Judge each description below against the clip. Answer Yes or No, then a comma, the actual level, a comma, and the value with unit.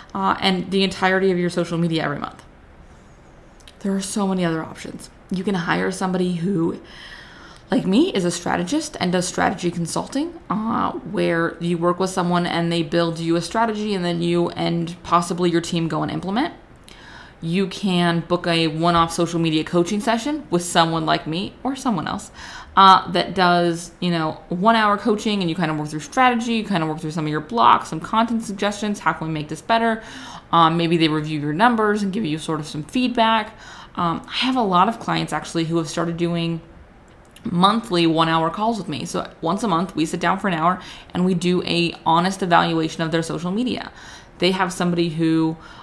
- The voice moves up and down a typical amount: Yes, average, 3.2 semitones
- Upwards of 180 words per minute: Yes, fast, 205 wpm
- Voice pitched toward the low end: No, medium, 175 Hz